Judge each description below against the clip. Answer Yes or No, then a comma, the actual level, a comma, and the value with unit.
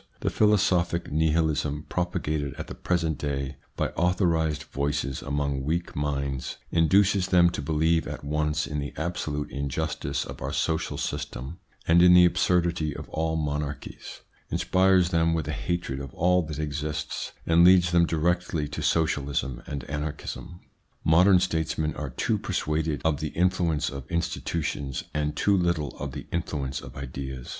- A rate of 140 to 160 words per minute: Yes, average, 150 wpm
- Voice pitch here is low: Yes, very low, 80 Hz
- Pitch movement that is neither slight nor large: Yes, average, 3.1 semitones